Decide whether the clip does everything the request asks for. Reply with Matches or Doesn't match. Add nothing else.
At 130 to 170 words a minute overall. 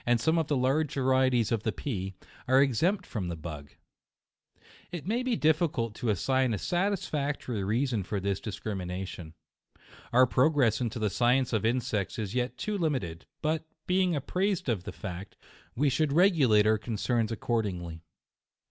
Matches